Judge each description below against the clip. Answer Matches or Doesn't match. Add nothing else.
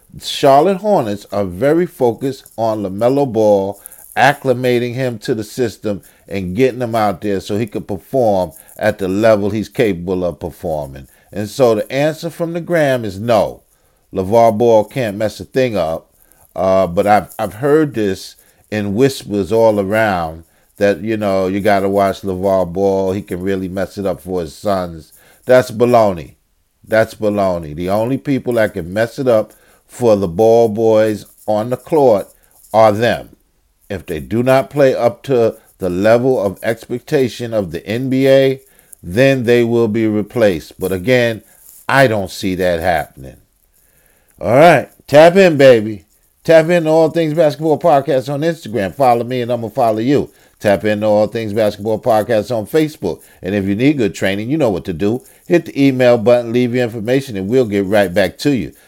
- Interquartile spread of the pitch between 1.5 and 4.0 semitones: Doesn't match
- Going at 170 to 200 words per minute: Matches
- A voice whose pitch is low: Matches